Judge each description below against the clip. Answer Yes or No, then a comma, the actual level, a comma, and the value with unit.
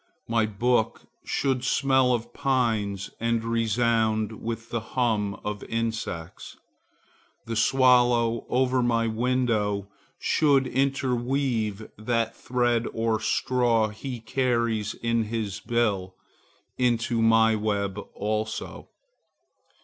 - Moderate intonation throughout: No, narrow, 2.2 semitones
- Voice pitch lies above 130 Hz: No, low, 115 Hz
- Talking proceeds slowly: Yes, slow, 100 wpm